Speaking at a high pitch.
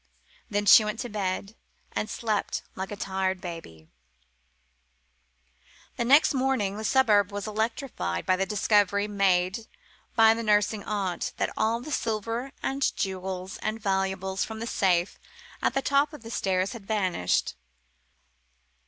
Yes: high, 205 Hz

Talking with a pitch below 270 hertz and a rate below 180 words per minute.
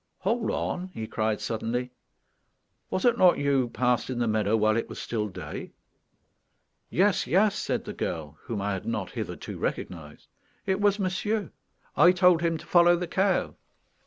Yes: low, 135 Hz; average, 170 wpm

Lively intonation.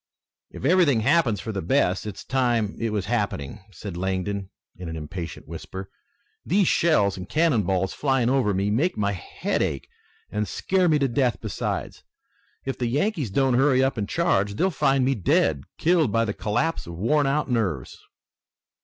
Yes: wide, 6.1 semitones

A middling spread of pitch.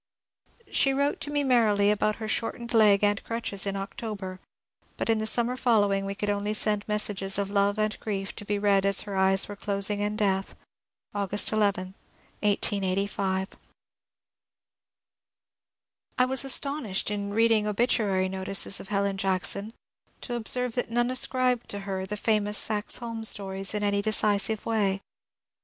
No: narrow, 2.1 semitones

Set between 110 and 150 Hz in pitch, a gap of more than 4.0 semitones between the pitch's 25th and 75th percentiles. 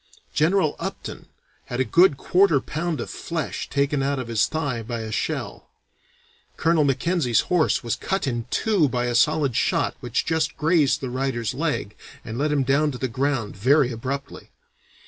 Yes: medium, 140 Hz; average, 4.4 semitones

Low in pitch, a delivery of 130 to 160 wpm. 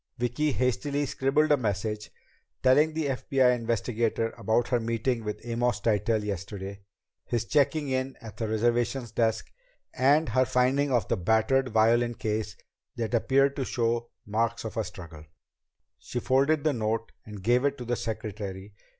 Yes: low, 120 Hz; average, 155 wpm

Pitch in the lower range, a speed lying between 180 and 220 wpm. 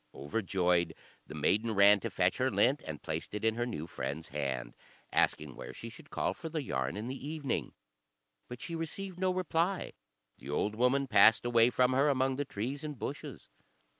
Yes: low, 120 Hz; average, 190 wpm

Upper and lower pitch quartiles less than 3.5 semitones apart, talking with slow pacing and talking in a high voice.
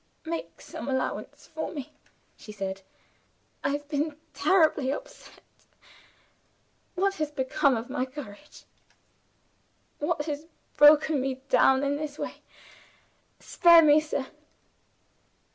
Yes: average, 2.8 semitones; slow, 110 wpm; very high, 290 Hz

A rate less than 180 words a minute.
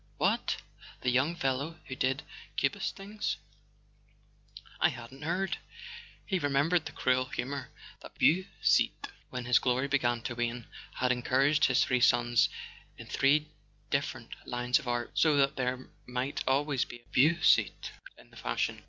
Yes: average, 145 wpm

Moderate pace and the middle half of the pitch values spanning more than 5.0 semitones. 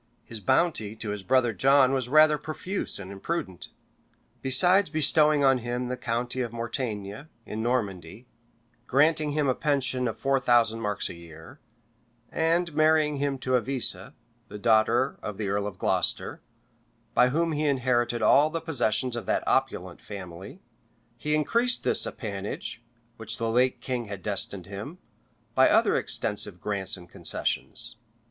Yes: average, 150 wpm; wide, 5.6 semitones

